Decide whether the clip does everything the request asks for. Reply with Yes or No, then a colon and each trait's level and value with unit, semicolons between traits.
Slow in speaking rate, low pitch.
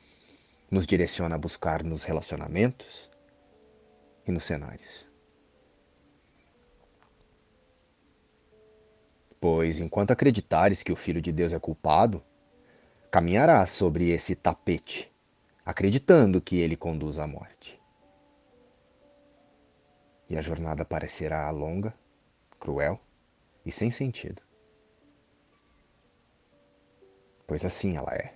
Yes: slow, 90 wpm; very low, 85 Hz